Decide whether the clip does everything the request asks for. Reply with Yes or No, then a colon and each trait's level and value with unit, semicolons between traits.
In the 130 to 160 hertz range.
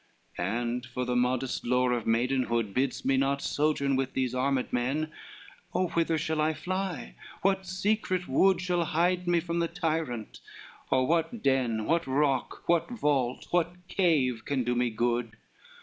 Yes: medium, 140 Hz